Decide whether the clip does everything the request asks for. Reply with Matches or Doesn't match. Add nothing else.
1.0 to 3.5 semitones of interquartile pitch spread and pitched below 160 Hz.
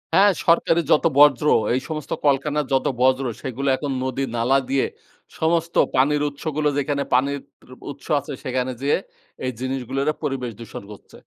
Matches